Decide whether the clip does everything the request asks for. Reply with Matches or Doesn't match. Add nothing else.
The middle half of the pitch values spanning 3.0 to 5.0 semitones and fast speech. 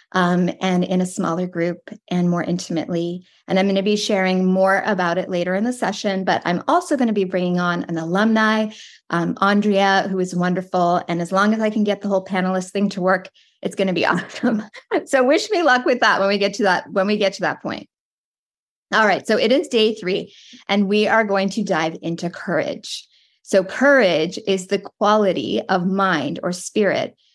Doesn't match